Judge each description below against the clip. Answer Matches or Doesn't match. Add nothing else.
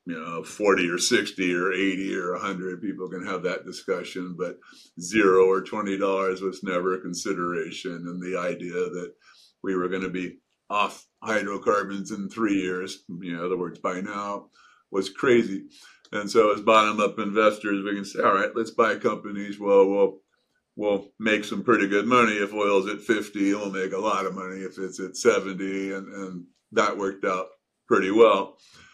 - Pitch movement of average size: Doesn't match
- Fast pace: Doesn't match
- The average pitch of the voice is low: Matches